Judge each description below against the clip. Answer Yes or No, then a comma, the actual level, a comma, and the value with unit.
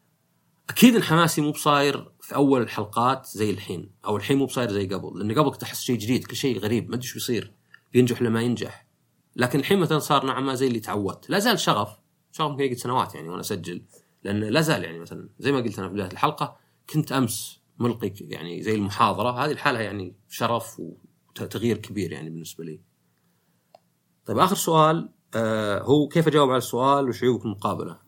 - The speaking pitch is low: Yes, low, 120 Hz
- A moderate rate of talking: No, fast, 185 wpm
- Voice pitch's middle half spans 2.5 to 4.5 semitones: No, average, 5.1 semitones